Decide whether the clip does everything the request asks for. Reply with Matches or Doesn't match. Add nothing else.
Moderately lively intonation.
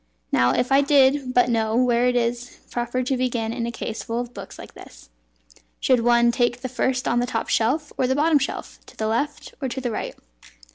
Doesn't match